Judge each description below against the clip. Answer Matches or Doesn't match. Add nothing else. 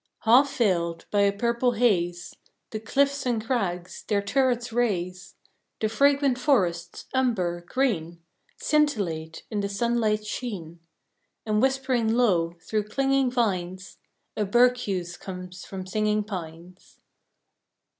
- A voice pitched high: Matches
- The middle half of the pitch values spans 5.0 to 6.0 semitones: Matches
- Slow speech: Matches